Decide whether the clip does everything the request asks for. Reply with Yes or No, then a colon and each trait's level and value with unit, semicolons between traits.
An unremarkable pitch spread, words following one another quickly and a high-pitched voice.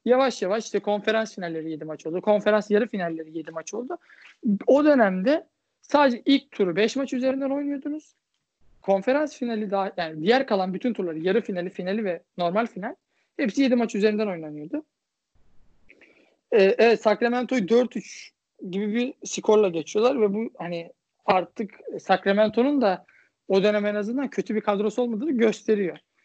Yes: average, 4.6 semitones; fast, 150 wpm; high, 215 Hz